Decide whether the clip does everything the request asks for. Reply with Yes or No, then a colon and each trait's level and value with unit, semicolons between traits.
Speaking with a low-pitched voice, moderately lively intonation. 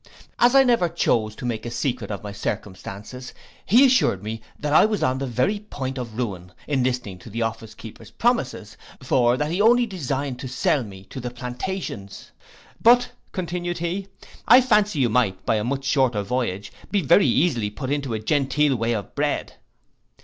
No: low, 130 Hz; wide, 7.6 semitones